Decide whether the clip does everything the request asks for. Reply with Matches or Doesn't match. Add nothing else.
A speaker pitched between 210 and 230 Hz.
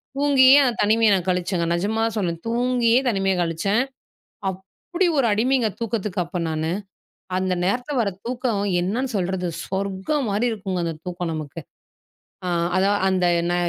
Doesn't match